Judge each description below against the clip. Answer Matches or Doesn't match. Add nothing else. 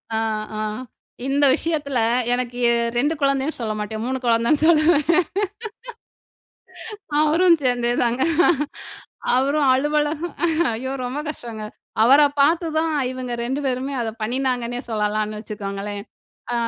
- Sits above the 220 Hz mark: Matches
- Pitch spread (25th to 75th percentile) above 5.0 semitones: Doesn't match